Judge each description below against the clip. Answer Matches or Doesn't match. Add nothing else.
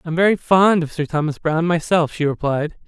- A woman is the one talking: Doesn't match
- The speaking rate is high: Matches